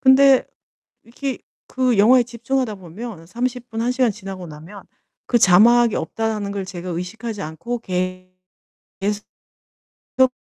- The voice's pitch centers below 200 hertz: No, high, 220 Hz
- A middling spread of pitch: Yes, average, 4.7 semitones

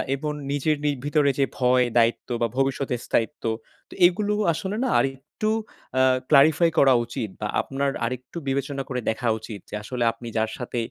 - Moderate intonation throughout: Yes, average, 3.2 semitones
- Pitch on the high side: No, low, 135 Hz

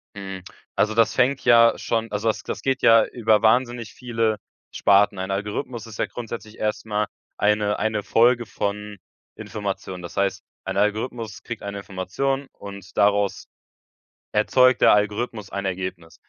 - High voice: No, low, 105 Hz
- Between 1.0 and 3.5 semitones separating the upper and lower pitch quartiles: Yes, narrow, 2.4 semitones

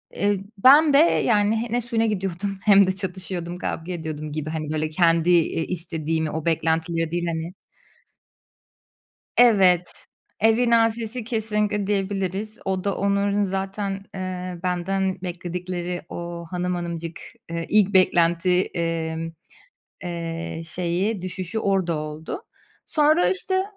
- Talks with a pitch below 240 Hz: Yes, medium, 185 Hz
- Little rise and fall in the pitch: No, average, 3.4 semitones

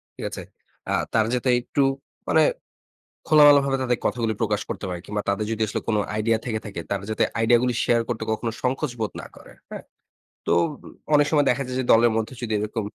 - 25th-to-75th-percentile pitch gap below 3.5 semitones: Yes, average, 2.9 semitones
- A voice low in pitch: Yes, low, 115 Hz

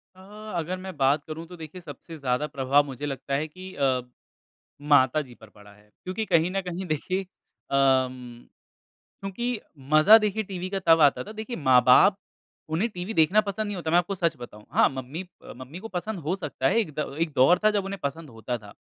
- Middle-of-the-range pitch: Yes, medium, 160 Hz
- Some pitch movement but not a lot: No, wide, 5.9 semitones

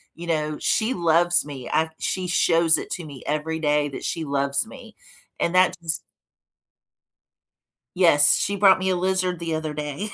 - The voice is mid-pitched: Yes, medium, 165 Hz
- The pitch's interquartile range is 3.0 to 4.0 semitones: Yes, average, 3.3 semitones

